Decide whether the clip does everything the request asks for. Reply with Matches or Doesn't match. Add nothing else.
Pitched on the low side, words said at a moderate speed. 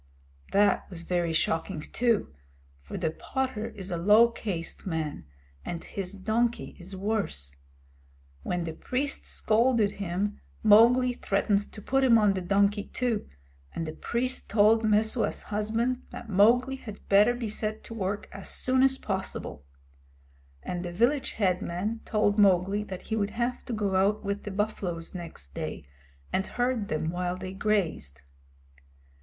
Doesn't match